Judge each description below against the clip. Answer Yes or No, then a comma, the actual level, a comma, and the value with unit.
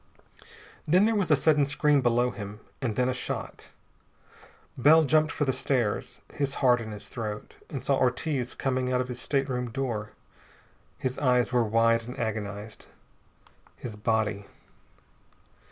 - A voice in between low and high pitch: No, low, 125 Hz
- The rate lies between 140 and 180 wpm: Yes, average, 150 wpm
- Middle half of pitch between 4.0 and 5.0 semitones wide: No, average, 3.5 semitones